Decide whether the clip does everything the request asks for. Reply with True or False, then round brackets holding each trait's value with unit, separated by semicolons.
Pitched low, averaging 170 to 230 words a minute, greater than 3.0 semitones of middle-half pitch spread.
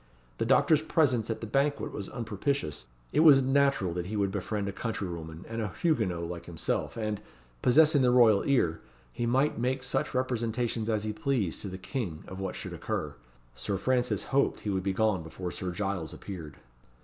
True (110 Hz; 185 wpm; 5.6 semitones)